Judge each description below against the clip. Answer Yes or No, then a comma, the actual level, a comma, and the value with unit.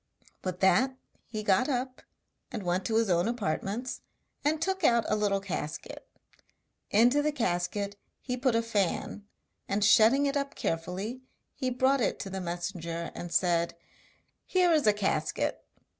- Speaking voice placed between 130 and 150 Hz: No, high, 210 Hz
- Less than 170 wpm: Yes, average, 155 wpm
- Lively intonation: Yes, wide, 5.7 semitones